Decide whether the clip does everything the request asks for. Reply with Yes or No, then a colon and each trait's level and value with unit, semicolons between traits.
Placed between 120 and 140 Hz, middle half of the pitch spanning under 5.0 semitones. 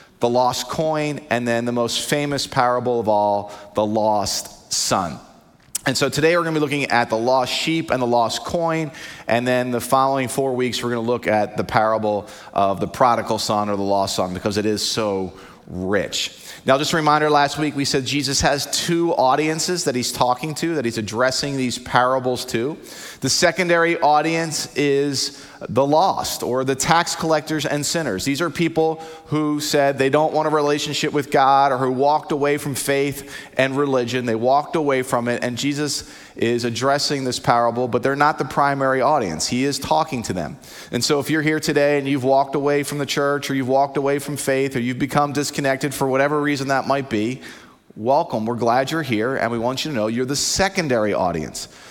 Yes: low, 135 Hz; average, 3.5 semitones